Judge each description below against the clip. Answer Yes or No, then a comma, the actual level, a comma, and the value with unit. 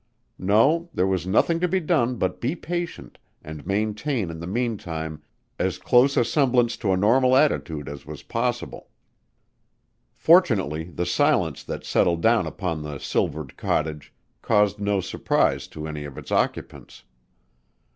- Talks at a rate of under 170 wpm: Yes, average, 145 wpm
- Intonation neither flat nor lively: No, wide, 7.9 semitones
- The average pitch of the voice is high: No, low, 100 Hz